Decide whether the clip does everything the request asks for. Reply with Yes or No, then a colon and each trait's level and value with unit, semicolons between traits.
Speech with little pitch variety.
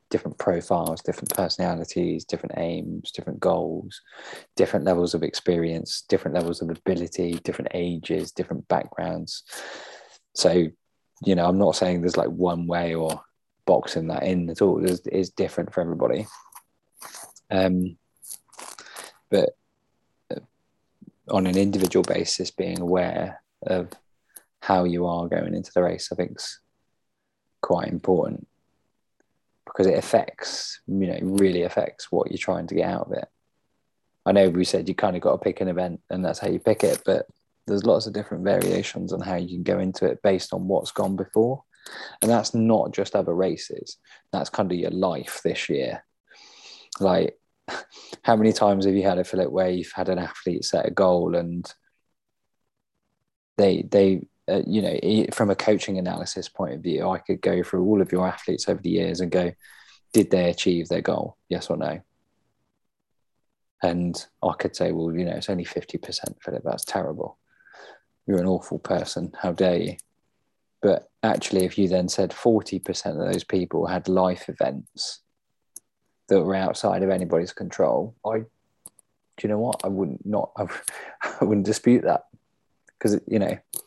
Yes: narrow, 1.8 semitones